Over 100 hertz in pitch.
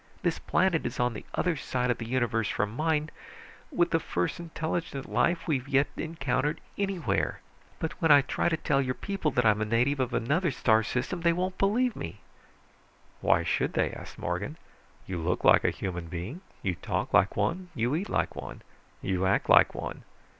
Yes: medium, 140 Hz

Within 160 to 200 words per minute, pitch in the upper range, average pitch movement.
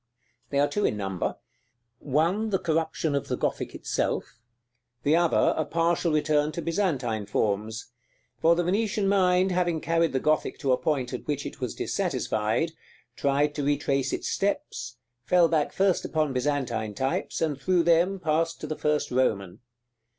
No: average, 165 wpm; medium, 155 Hz; average, 4.5 semitones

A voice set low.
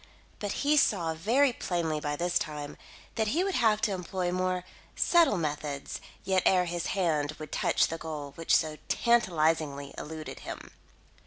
No: medium, 175 Hz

